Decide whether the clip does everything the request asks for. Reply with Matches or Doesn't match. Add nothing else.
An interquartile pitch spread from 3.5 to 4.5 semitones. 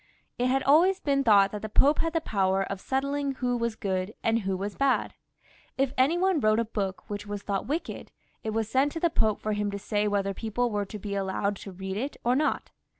Doesn't match